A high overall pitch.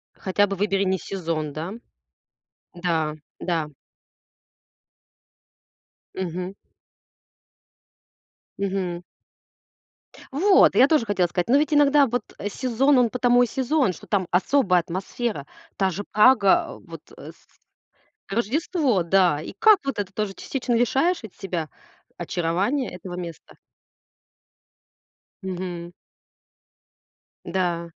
Yes: high, 195 Hz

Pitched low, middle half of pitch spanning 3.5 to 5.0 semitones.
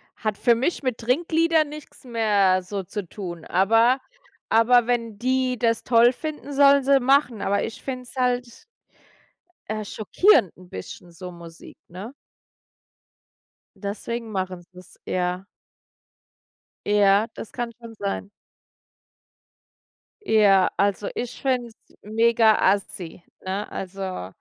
No: high, 225 Hz; average, 4.3 semitones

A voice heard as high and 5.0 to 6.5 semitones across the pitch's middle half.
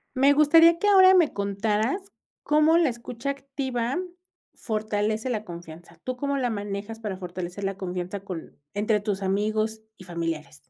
Yes: high, 215 Hz; wide, 5.6 semitones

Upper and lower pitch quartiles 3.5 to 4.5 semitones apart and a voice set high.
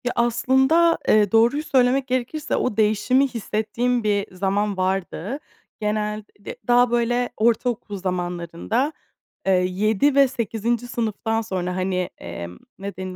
Yes: average, 4.2 semitones; high, 220 Hz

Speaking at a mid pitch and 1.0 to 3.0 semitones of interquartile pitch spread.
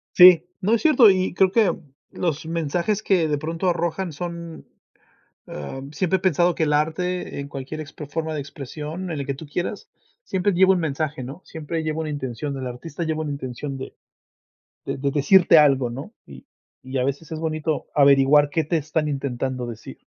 No: medium, 155 Hz; average, 3.7 semitones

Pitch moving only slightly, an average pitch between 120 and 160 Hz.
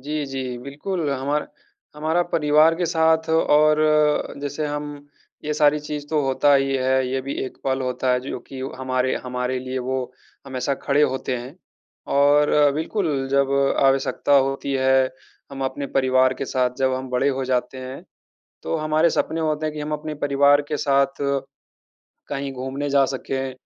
Yes: narrow, 2.3 semitones; medium, 140 Hz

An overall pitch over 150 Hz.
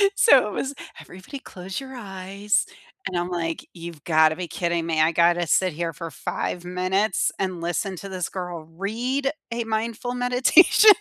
Yes: medium, 185 Hz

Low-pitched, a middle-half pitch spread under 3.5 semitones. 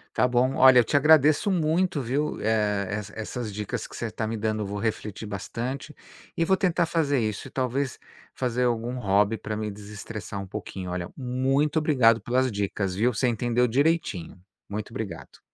No: low, 115 Hz; average, 4.4 semitones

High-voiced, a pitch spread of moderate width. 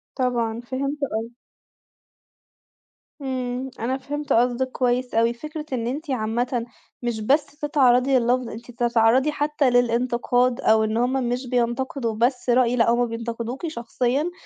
No: high, 245 Hz; narrow, 2.0 semitones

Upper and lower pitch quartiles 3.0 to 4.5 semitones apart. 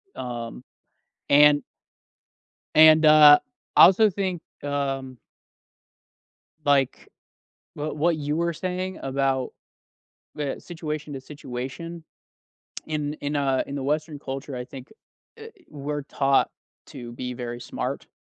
No: narrow, 2.6 semitones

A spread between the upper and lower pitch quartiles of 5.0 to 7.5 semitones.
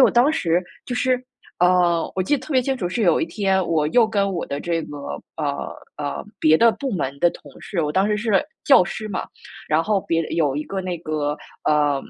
Yes: wide, 5.5 semitones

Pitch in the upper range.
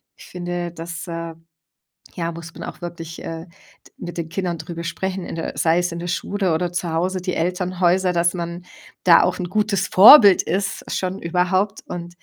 No: medium, 175 Hz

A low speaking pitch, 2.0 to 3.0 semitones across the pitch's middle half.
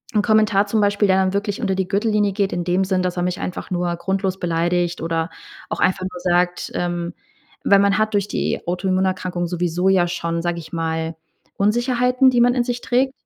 No: medium, 185 Hz; average, 2.7 semitones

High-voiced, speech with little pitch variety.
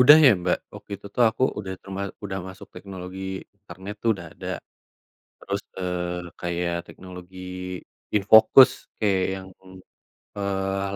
No: very low, 95 Hz; narrow, 1.8 semitones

